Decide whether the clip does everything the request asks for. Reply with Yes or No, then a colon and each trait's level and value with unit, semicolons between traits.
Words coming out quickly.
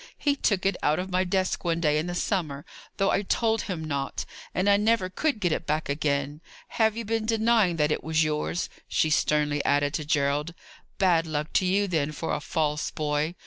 Yes: fast, 210 wpm